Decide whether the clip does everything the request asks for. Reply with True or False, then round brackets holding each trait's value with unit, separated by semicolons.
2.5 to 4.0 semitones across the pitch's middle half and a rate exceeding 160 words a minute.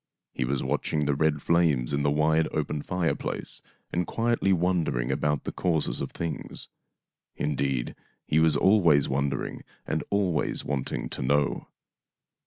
False (3.1 semitones; 150 wpm)